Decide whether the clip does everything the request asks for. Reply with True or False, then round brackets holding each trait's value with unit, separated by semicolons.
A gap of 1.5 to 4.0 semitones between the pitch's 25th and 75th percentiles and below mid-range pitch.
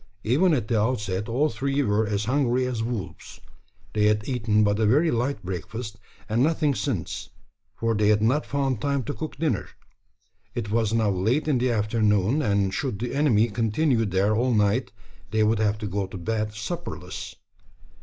True (3.7 semitones; 110 Hz)